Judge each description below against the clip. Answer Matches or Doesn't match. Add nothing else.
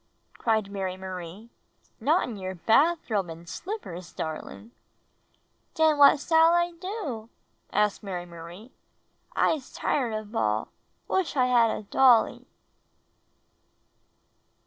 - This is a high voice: Matches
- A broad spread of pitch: Matches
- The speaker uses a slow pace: Matches